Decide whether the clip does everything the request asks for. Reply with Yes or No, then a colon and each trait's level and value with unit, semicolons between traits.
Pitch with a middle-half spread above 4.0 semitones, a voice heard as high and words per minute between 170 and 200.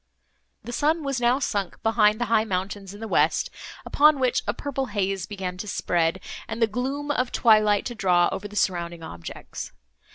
Yes: average, 4.5 semitones; high, 215 Hz; average, 185 wpm